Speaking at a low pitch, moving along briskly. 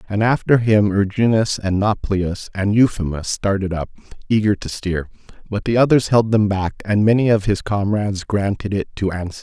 No: low, 105 Hz; average, 180 wpm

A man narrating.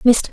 No: female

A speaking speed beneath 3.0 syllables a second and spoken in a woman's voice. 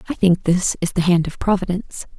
No: 6.0 syllables/s; female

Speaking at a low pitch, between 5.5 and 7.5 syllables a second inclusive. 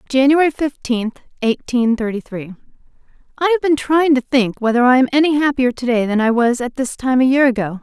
No: very high, 255 Hz; 5.6 syllables/s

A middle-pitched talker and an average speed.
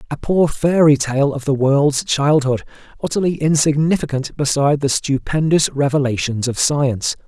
No: medium, 145 Hz; slow, 130 wpm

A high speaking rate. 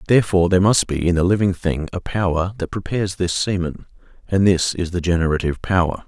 No: average, 195 wpm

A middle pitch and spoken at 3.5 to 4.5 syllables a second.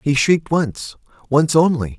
Yes: medium, 145 Hz; 4.3 syllables/s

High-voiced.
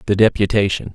No: low, 105 Hz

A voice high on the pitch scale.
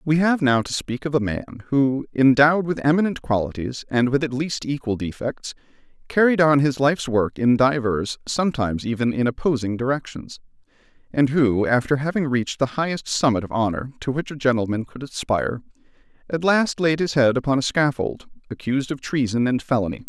No: low, 135 Hz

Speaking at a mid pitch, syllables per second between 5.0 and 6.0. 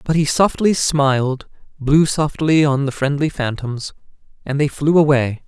No: medium, 145 Hz; 4.4 syllables/s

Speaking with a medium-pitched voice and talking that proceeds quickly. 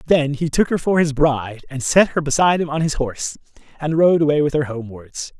Yes: medium, 145 Hz; fast, 235 wpm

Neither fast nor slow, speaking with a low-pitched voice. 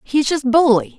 No: average, 185 wpm; very high, 280 Hz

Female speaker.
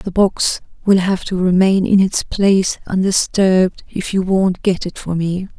Yes: female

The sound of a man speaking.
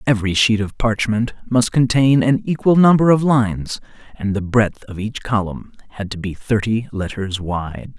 Yes: male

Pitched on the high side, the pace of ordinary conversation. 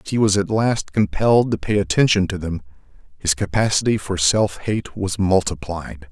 No: very low, 95 Hz; average, 175 wpm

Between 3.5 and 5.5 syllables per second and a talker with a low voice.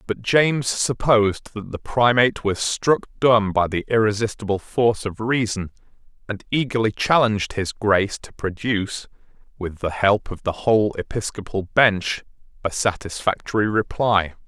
Yes: 4.8 syllables/s; low, 105 Hz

